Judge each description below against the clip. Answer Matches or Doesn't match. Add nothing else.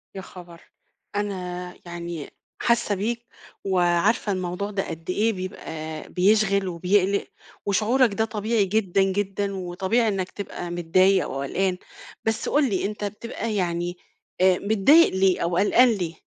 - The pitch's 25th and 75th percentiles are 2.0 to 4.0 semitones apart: Matches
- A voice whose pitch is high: Matches